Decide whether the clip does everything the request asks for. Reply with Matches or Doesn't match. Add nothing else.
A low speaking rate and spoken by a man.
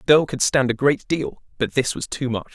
Doesn't match